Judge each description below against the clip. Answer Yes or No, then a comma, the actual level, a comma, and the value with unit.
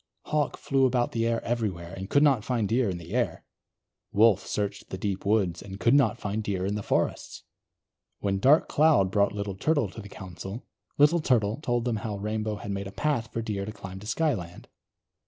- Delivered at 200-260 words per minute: Yes, fast, 205 wpm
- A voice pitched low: Yes, low, 105 Hz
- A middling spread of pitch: Yes, average, 3.7 semitones